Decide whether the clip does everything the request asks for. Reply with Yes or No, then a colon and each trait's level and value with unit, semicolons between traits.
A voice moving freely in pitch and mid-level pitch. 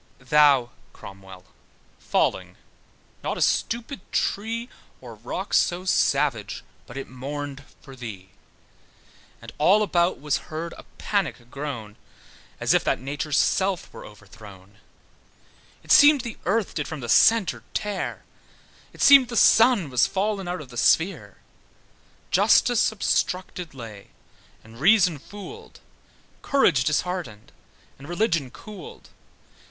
Yes: wide, 8.3 semitones; medium, 155 Hz